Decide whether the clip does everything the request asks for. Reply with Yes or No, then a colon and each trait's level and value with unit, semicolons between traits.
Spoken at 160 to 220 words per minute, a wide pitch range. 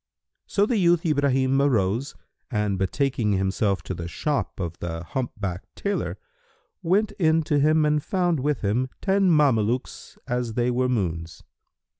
No: average, 145 wpm; wide, 7.3 semitones